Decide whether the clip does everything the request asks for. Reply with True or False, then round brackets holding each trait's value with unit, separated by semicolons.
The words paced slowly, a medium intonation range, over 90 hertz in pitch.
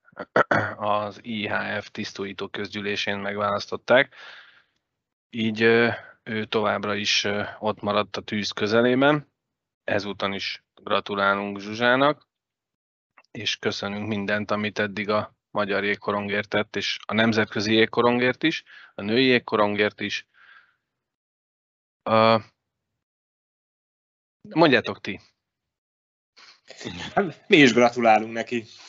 False (85 wpm; 1.9 semitones; 105 Hz)